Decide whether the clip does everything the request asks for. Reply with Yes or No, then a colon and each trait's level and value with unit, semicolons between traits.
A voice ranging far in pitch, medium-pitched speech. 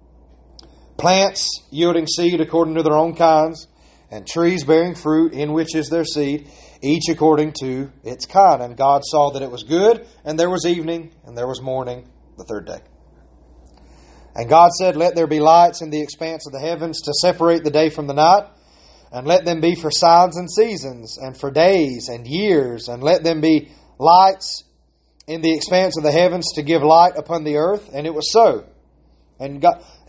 No: average, 4.5 semitones; medium, 155 Hz